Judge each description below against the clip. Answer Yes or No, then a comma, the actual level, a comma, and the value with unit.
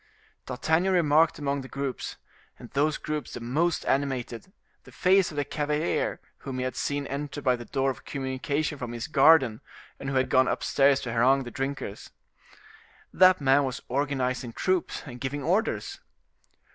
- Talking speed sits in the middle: Yes, average, 165 wpm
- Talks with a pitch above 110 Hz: Yes, medium, 140 Hz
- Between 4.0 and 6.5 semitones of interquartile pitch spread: No, narrow, 2.5 semitones